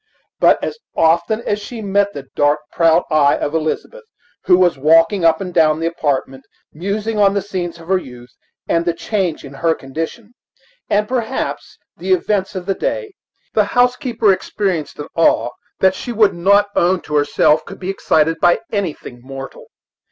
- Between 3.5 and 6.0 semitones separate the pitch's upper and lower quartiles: Yes, average, 4.5 semitones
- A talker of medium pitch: Yes, medium, 175 Hz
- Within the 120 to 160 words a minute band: No, average, 175 wpm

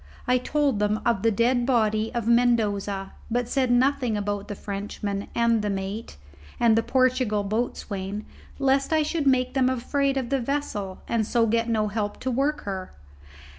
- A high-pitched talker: Yes, high, 230 Hz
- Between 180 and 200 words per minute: No, average, 170 wpm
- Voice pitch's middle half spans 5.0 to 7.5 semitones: No, average, 3.8 semitones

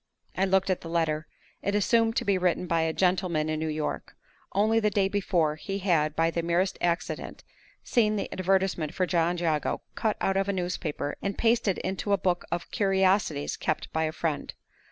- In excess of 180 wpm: Yes, average, 195 wpm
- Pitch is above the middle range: No, medium, 180 Hz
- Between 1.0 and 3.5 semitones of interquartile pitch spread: Yes, average, 3.2 semitones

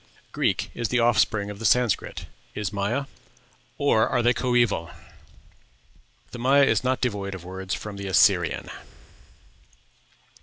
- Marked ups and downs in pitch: No, average, 3.8 semitones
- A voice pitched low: Yes, low, 110 Hz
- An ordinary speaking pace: No, slow, 130 wpm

